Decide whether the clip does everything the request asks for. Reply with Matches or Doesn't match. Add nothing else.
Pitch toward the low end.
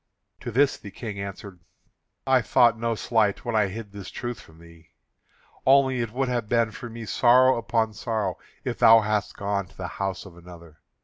Matches